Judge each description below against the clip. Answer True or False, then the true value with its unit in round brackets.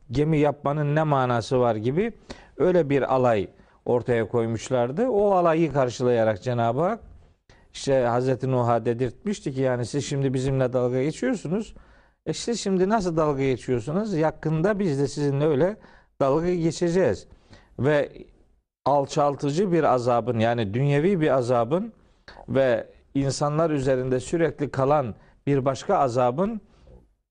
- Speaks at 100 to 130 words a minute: True (125 wpm)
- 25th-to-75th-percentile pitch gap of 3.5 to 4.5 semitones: False (5.0 semitones)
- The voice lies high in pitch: False (140 Hz)